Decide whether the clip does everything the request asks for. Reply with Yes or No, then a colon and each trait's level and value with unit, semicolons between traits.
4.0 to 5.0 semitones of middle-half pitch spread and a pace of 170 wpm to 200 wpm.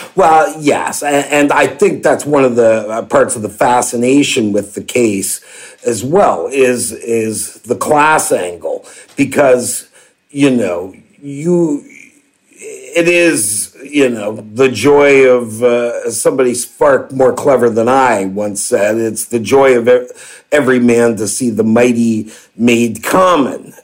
No: average, 4.4 semitones; average, 140 wpm